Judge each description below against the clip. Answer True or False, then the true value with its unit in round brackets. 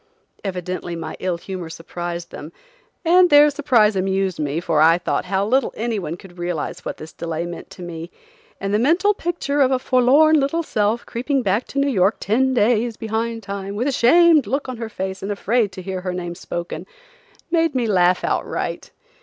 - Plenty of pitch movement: True (6.5 semitones)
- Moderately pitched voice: False (205 Hz)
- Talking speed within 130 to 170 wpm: False (190 wpm)